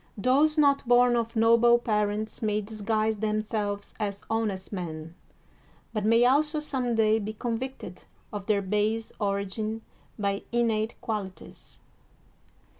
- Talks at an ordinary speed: No, slow, 125 wpm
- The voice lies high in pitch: Yes, high, 220 Hz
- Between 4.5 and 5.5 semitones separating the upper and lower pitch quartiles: No, narrow, 2.5 semitones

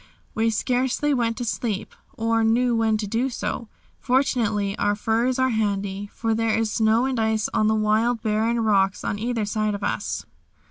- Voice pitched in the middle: No, high, 225 Hz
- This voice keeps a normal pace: Yes, average, 180 wpm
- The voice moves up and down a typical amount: No, narrow, 1.9 semitones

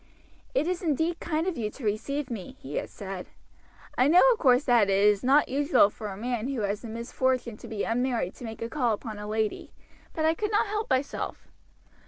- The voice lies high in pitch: Yes, high, 245 Hz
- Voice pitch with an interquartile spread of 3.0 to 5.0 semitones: No, wide, 5.6 semitones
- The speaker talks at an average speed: No, fast, 220 wpm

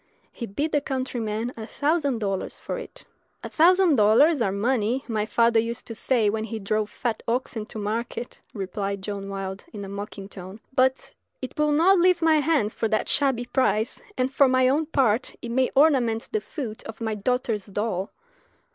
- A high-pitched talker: Yes, high, 230 Hz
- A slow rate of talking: No, average, 185 wpm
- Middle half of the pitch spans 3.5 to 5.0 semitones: Yes, average, 4.2 semitones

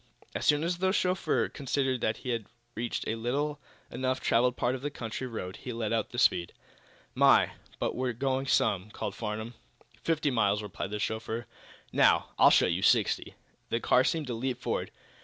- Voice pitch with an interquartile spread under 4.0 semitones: Yes, average, 3.4 semitones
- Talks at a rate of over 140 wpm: Yes, average, 185 wpm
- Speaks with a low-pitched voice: Yes, low, 120 Hz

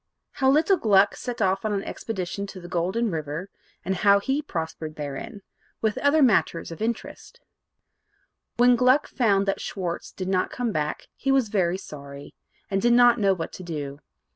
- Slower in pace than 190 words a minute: Yes, average, 175 wpm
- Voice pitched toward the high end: Yes, high, 195 Hz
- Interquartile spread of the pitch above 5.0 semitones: Yes, wide, 5.5 semitones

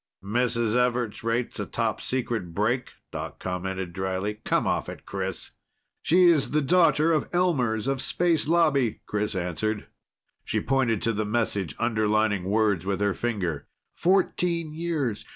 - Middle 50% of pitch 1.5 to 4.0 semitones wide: No, wide, 5.4 semitones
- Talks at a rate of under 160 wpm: Yes, slow, 135 wpm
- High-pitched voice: No, low, 115 Hz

